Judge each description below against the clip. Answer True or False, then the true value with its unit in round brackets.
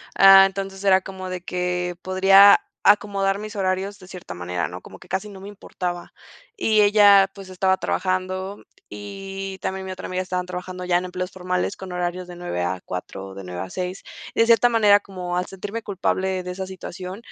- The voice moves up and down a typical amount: False (1.4 semitones)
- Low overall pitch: False (185 Hz)